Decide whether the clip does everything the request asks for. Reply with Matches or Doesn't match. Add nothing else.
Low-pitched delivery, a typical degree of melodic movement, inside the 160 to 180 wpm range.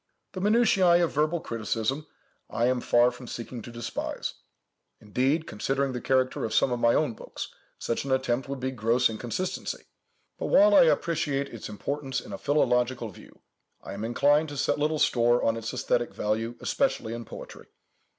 Matches